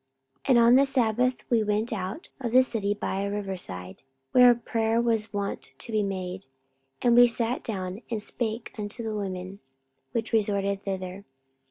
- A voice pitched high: Yes, high, 215 Hz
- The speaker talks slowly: No, average, 175 wpm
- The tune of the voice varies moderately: Yes, average, 3.1 semitones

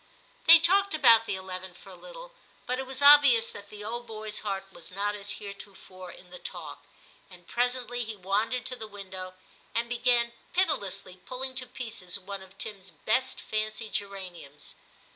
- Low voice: No, high, 215 Hz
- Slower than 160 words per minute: No, average, 175 wpm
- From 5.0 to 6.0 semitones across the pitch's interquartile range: No, average, 4.5 semitones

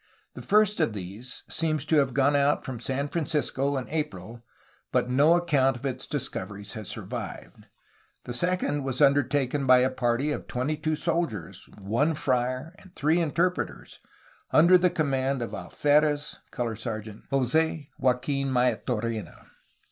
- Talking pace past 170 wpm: No, average, 145 wpm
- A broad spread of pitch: No, average, 3.8 semitones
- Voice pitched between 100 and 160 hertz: Yes, low, 135 Hz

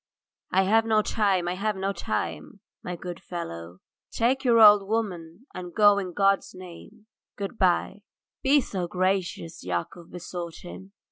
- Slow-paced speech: No, average, 145 wpm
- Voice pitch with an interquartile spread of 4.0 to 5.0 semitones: No, average, 3.2 semitones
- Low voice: No, high, 190 Hz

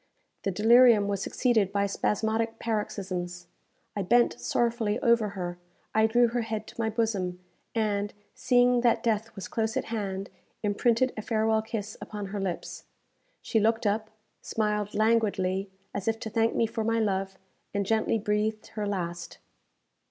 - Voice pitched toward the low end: No, high, 215 Hz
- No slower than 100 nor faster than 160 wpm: Yes, average, 155 wpm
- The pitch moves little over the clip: Yes, narrow, 2.1 semitones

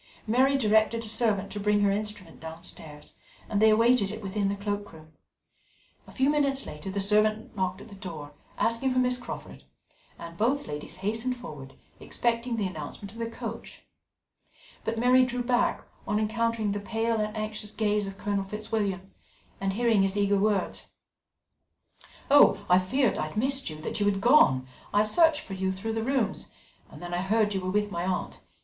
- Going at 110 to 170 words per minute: No, average, 180 wpm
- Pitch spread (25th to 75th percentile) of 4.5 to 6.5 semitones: No, average, 3.1 semitones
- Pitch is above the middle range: Yes, high, 210 Hz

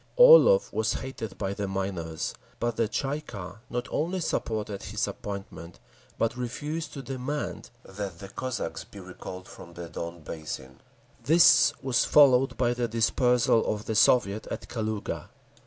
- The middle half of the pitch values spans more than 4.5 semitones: Yes, average, 5.3 semitones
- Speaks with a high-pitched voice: No, low, 110 Hz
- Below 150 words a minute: No, average, 155 wpm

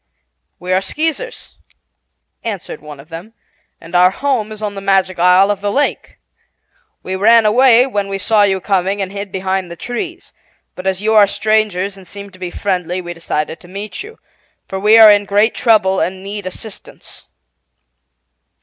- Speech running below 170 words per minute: No, average, 175 wpm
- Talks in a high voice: Yes, high, 195 Hz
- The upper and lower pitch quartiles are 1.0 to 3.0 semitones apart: Yes, narrow, 2.6 semitones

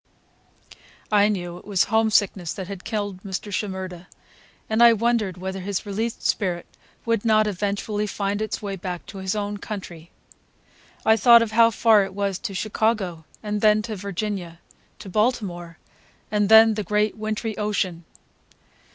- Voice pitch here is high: Yes, high, 205 Hz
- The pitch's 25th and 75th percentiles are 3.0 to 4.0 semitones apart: No, narrow, 2.4 semitones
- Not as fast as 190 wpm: Yes, average, 150 wpm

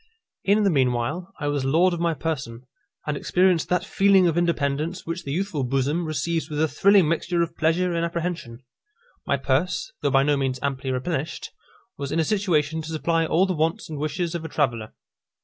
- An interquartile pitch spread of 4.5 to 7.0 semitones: No, average, 3.8 semitones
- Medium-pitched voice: Yes, medium, 160 Hz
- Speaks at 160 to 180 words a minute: No, average, 195 wpm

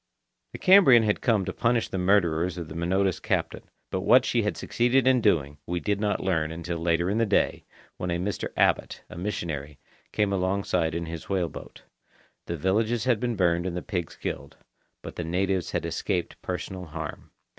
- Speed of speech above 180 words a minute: Yes, average, 190 wpm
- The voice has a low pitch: Yes, very low, 95 Hz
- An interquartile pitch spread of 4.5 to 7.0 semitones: No, average, 3.7 semitones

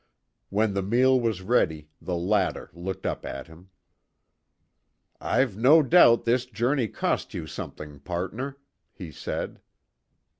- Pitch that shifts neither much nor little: No, wide, 5.9 semitones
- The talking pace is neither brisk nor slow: No, slow, 125 wpm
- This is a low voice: Yes, low, 105 Hz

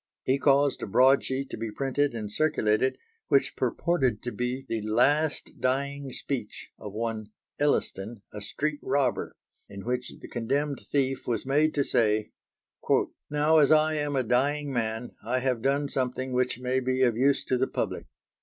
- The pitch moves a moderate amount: Yes, average, 3.3 semitones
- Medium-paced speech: Yes, average, 170 wpm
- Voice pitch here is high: No, low, 130 Hz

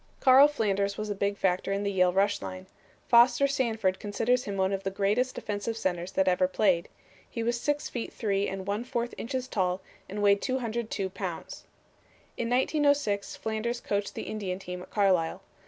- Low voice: No, high, 205 Hz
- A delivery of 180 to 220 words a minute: Yes, average, 185 wpm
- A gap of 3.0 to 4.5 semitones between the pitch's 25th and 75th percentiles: Yes, average, 3.6 semitones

